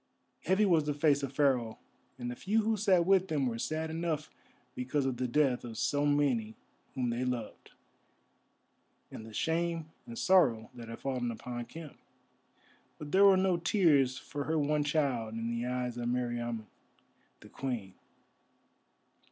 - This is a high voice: No, medium, 140 Hz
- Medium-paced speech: Yes, average, 160 wpm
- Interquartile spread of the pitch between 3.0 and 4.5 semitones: No, average, 5.1 semitones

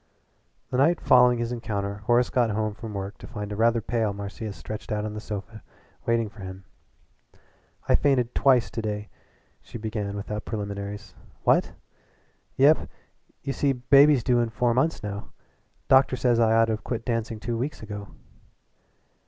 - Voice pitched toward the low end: Yes, low, 115 Hz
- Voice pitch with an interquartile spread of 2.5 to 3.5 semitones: Yes, average, 2.8 semitones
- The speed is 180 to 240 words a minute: No, average, 170 wpm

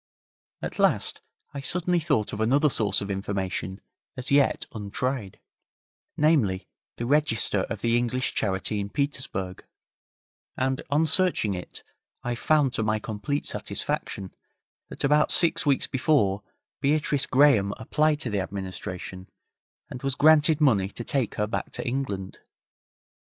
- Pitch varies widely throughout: Yes, wide, 6.3 semitones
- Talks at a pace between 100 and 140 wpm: Yes, slow, 135 wpm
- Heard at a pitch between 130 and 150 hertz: No, low, 120 Hz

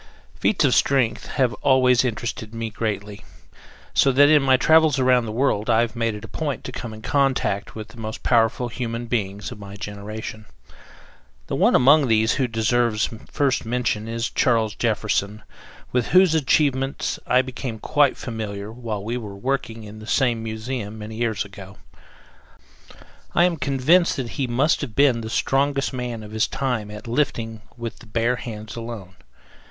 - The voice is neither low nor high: No, low, 115 Hz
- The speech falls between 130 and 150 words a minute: No, average, 170 wpm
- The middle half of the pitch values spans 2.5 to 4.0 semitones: Yes, average, 3.3 semitones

